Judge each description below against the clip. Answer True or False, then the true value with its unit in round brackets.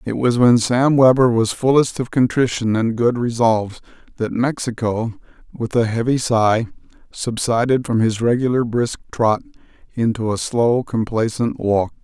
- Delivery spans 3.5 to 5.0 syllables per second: True (4.5 syllables/s)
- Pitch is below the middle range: True (115 Hz)